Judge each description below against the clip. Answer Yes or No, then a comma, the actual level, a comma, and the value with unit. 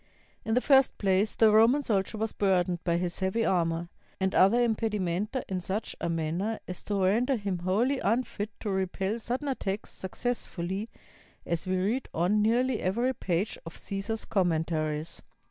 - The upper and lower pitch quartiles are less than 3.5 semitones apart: No, average, 3.8 semitones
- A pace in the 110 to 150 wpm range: No, average, 165 wpm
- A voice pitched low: No, high, 195 Hz